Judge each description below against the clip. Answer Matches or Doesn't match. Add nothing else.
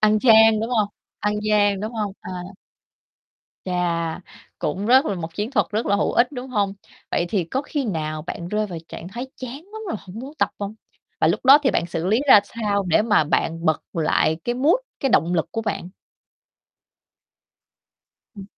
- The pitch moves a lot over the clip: Doesn't match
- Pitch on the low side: Doesn't match